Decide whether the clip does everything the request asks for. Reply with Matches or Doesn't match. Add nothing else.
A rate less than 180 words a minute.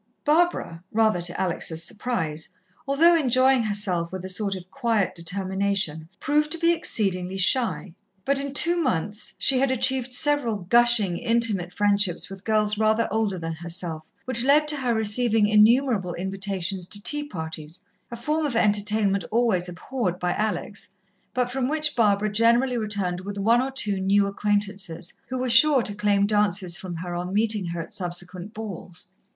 Matches